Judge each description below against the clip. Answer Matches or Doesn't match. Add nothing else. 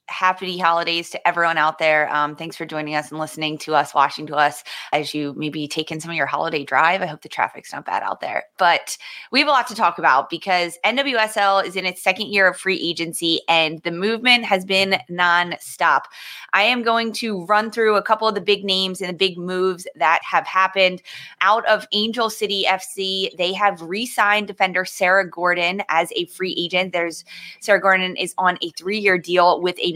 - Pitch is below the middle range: Doesn't match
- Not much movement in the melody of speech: Doesn't match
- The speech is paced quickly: Matches